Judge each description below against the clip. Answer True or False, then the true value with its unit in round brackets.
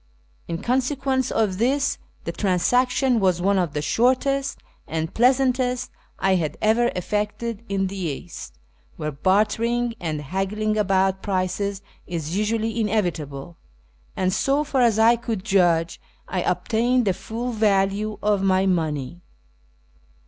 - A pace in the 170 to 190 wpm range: False (135 wpm)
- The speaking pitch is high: True (205 Hz)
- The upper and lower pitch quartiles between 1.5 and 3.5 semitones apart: False (4.5 semitones)